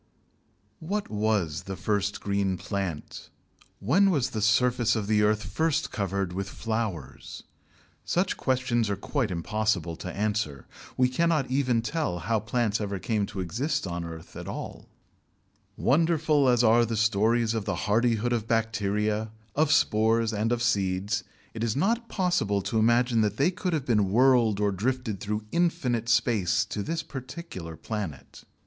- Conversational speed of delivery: Yes, average, 155 wpm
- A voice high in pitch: No, low, 110 Hz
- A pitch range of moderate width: Yes, average, 4.0 semitones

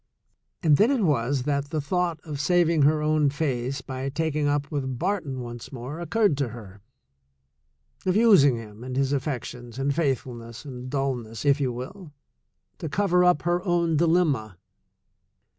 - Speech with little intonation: No, average, 4.4 semitones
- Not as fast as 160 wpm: No, average, 165 wpm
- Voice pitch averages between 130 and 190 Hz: Yes, medium, 140 Hz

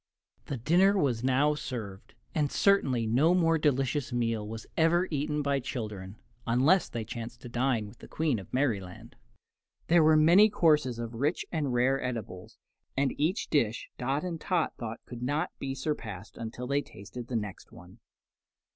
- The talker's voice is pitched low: Yes, low, 130 Hz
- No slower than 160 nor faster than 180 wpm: Yes, average, 165 wpm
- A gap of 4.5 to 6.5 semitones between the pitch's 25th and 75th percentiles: Yes, average, 5.0 semitones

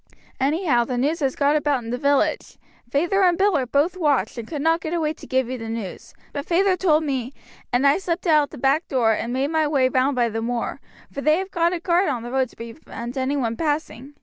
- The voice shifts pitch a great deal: No, average, 4.5 semitones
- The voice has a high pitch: Yes, very high, 280 Hz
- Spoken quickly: Yes, fast, 250 wpm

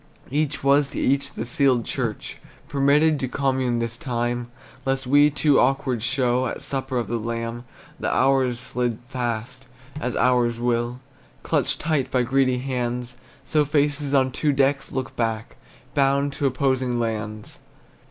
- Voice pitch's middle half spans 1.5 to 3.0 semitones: Yes, narrow, 2.5 semitones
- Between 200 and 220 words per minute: No, average, 150 wpm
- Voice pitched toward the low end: Yes, low, 130 Hz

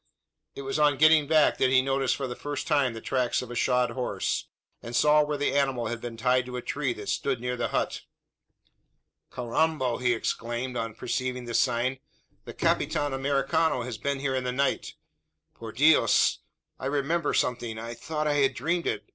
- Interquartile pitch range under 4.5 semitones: Yes, average, 2.8 semitones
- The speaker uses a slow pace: No, average, 190 wpm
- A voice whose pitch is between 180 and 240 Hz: No, low, 130 Hz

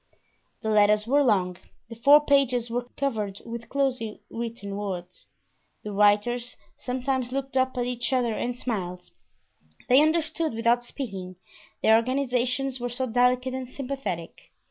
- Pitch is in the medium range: No, high, 245 Hz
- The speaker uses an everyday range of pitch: Yes, average, 3.5 semitones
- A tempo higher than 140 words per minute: No, slow, 135 wpm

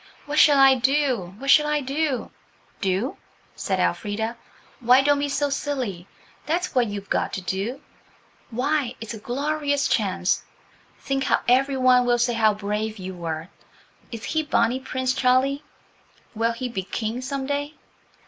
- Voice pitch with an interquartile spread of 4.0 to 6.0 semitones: Yes, average, 4.4 semitones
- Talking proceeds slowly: No, average, 160 wpm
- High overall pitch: Yes, very high, 255 Hz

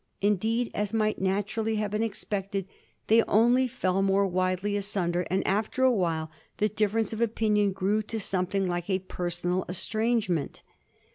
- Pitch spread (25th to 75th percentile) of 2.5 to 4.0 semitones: Yes, average, 2.8 semitones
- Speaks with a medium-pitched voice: No, high, 200 Hz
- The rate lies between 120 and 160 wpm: Yes, average, 150 wpm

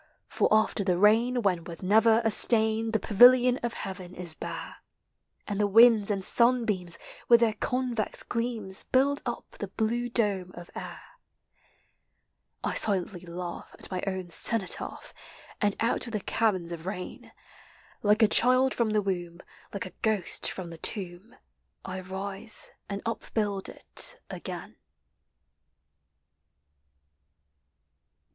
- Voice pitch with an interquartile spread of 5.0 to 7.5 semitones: No, average, 3.7 semitones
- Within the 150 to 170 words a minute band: No, slow, 135 wpm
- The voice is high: Yes, high, 210 Hz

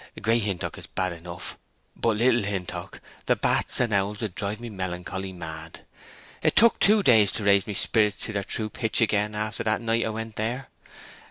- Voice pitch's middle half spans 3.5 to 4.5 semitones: No, average, 2.8 semitones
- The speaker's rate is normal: Yes, average, 180 wpm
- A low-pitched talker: Yes, low, 105 Hz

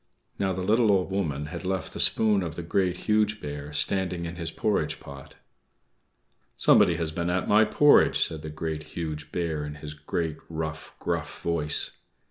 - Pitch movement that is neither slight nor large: Yes, average, 3.7 semitones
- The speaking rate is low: No, average, 175 wpm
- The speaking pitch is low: Yes, very low, 85 Hz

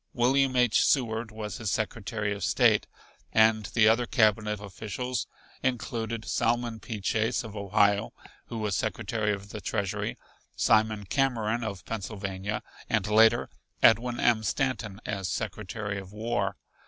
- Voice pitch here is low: Yes, low, 110 Hz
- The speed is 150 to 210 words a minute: No, slow, 135 wpm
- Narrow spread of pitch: Yes, narrow, 2.1 semitones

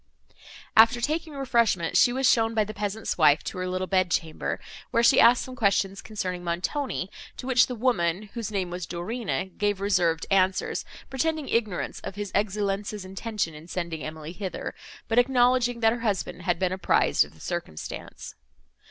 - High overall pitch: Yes, high, 205 Hz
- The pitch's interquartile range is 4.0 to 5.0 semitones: Yes, average, 4.5 semitones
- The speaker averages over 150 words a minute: Yes, average, 170 wpm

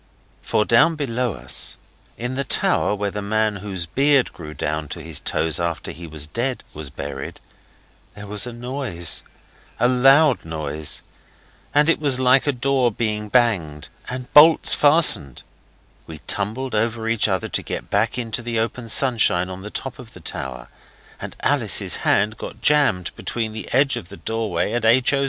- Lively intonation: Yes, wide, 6.0 semitones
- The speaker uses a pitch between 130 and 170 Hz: No, low, 110 Hz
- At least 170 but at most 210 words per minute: Yes, average, 175 wpm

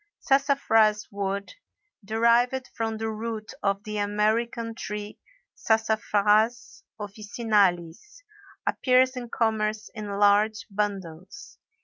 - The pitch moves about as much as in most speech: No, narrow, 2.1 semitones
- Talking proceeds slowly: Yes, slow, 90 wpm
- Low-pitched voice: No, high, 215 Hz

